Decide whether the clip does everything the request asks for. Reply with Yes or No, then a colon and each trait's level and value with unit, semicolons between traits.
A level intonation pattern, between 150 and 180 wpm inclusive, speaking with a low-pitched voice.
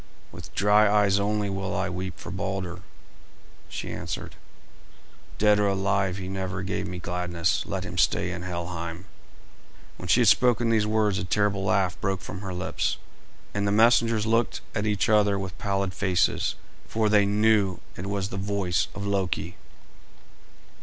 Yes: narrow, 2.1 semitones; average, 160 wpm; low, 100 Hz